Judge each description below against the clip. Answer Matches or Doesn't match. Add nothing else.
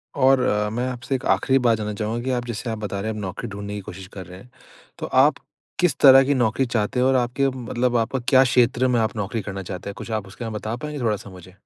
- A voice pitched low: Matches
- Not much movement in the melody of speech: Doesn't match